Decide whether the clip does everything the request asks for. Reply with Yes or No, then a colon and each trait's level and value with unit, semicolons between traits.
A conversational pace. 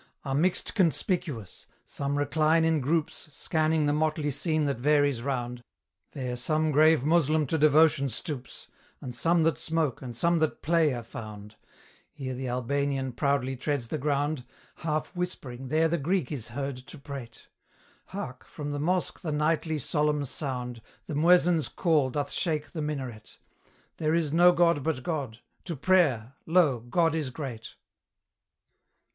Yes: average, 150 wpm